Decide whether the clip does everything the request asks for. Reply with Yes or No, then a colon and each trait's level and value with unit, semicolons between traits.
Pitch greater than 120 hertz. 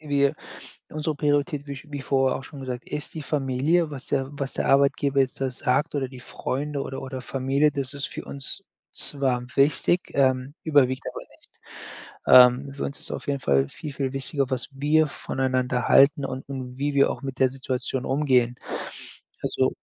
Yes: low, 135 Hz